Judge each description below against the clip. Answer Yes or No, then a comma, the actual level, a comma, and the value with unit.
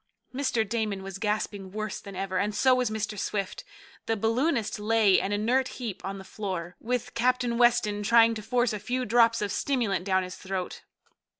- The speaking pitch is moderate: No, high, 215 Hz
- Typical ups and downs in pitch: Yes, average, 3.3 semitones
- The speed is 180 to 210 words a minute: Yes, average, 185 wpm